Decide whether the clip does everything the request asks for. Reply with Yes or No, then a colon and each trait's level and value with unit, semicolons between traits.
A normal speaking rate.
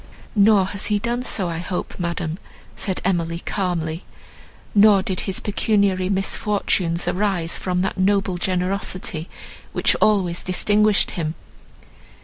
No: slow, 125 wpm